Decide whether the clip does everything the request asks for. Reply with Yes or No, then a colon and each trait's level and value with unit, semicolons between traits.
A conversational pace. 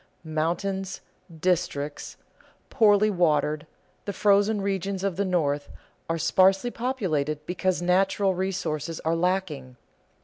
No: slow, 105 wpm